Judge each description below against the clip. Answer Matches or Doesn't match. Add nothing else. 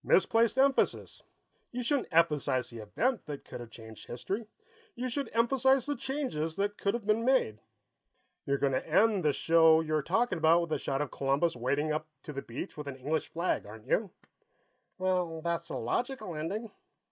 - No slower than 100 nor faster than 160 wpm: Doesn't match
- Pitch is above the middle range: Doesn't match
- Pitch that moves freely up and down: Matches